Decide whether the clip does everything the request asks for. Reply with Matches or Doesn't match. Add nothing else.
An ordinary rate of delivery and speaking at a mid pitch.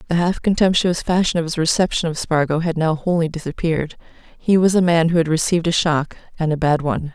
Doesn't match